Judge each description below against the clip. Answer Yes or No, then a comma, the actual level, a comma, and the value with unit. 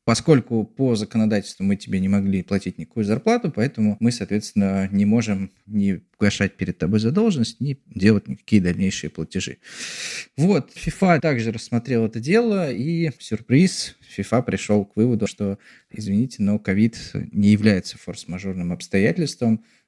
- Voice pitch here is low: Yes, low, 105 Hz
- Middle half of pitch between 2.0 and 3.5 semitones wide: Yes, average, 3.1 semitones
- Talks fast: No, average, 140 wpm